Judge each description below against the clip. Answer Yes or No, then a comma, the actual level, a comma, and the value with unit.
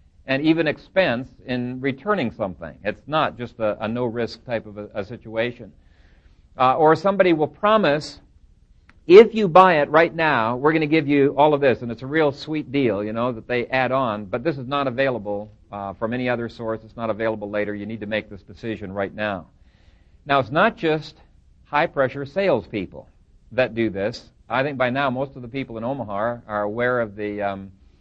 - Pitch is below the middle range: Yes, low, 120 Hz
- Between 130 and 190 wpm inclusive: No, fast, 205 wpm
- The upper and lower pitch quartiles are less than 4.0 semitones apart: No, wide, 5.4 semitones